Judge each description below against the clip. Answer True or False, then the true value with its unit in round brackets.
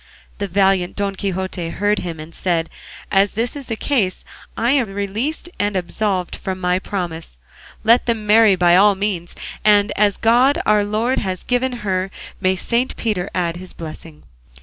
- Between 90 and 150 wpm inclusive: False (170 wpm)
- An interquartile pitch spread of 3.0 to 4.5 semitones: True (3.3 semitones)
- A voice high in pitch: True (200 Hz)